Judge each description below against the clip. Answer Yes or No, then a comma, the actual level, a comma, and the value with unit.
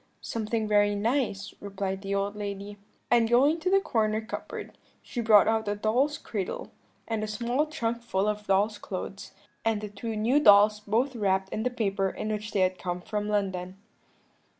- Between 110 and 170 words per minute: No, average, 180 wpm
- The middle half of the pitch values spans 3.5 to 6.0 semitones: No, narrow, 2.4 semitones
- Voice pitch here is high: Yes, high, 210 Hz